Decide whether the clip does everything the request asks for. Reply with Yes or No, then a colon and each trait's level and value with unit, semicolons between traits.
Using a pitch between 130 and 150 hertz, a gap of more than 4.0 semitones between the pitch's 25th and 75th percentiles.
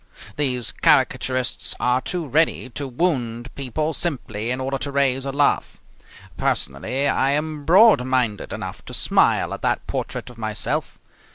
No: low, 135 Hz; average, 3.0 semitones